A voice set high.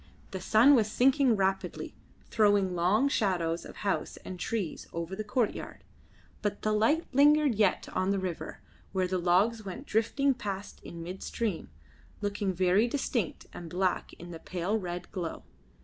Yes: high, 200 Hz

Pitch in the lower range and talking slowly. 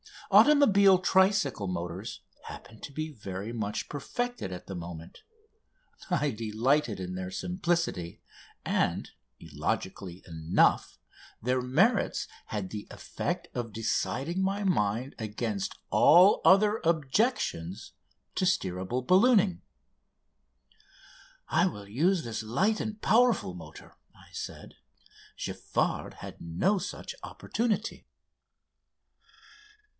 Yes: low, 130 Hz; slow, 100 wpm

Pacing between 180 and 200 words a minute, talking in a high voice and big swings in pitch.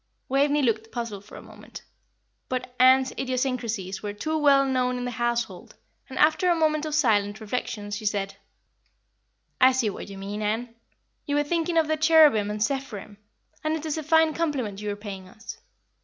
Yes: average, 185 wpm; very high, 250 Hz; wide, 6.0 semitones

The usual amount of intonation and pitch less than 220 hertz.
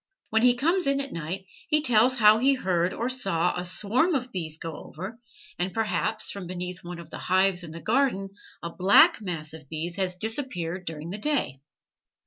No: wide, 6.0 semitones; high, 190 Hz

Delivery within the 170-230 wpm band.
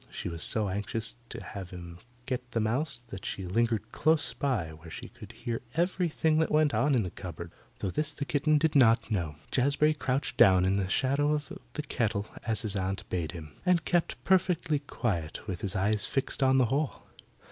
Yes: average, 200 wpm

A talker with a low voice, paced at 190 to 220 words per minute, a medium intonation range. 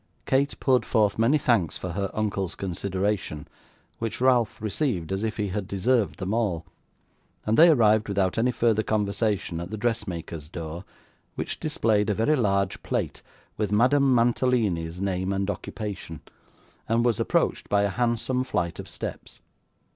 No: low, 105 Hz; average, 155 wpm; average, 3.6 semitones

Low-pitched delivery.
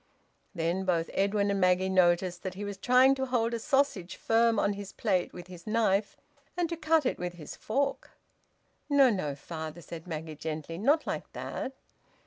No: high, 195 Hz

